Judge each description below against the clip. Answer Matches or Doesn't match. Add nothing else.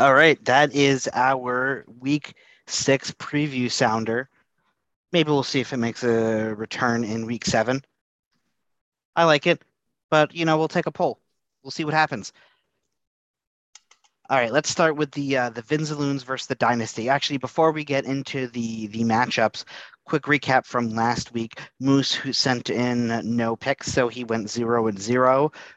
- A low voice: Matches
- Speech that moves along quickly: Doesn't match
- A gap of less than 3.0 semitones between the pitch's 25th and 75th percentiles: Doesn't match